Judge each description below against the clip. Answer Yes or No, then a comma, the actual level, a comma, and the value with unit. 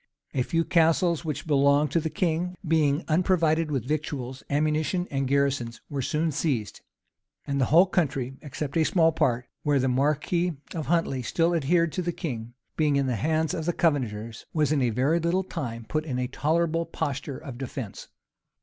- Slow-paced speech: No, average, 180 wpm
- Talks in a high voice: No, medium, 150 Hz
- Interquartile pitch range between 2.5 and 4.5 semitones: Yes, average, 3.7 semitones